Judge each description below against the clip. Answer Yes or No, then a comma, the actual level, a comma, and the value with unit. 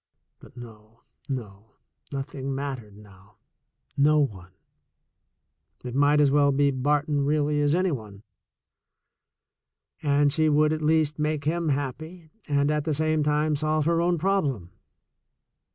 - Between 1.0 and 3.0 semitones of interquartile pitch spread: Yes, average, 2.7 semitones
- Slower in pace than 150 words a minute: Yes, average, 140 wpm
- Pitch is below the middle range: No, medium, 145 Hz